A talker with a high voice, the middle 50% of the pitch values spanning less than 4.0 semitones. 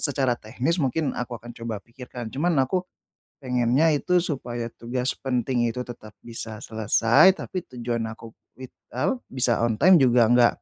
No: low, 125 Hz; average, 2.8 semitones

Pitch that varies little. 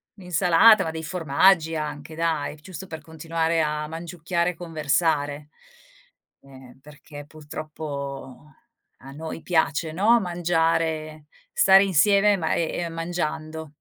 Yes: narrow, 2.3 semitones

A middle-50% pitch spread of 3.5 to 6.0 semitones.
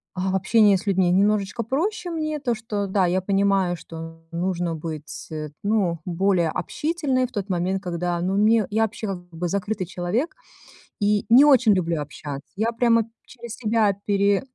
Yes: average, 4.2 semitones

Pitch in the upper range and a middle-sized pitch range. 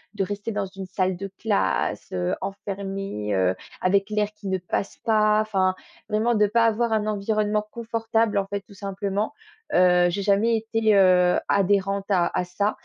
No: high, 200 Hz; narrow, 2.1 semitones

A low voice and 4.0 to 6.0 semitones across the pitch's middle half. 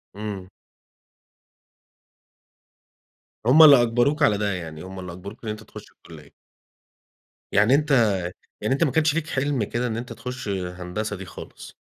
Yes: low, 110 Hz; wide, 5.6 semitones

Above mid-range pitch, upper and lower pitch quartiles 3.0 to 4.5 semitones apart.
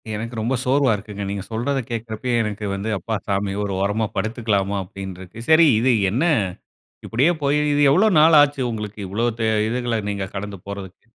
No: low, 110 Hz; average, 4.2 semitones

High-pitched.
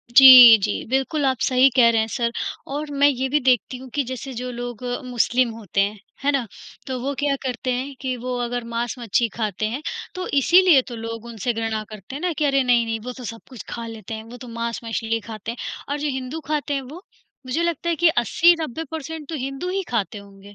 Yes: very high, 250 Hz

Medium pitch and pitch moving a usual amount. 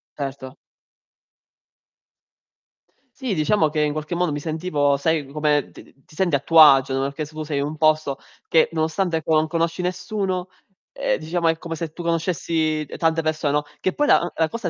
No: medium, 160 Hz; narrow, 2.1 semitones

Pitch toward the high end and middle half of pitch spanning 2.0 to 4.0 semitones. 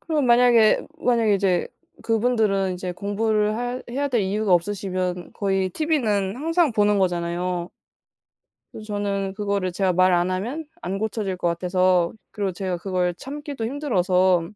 Yes: high, 200 Hz; average, 3.7 semitones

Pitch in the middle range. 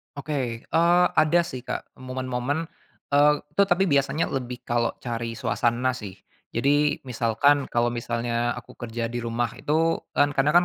No: low, 130 Hz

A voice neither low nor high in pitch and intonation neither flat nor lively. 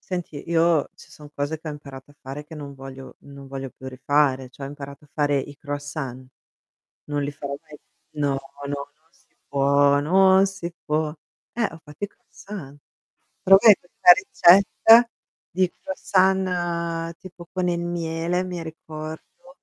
Yes: medium, 155 Hz; average, 3.7 semitones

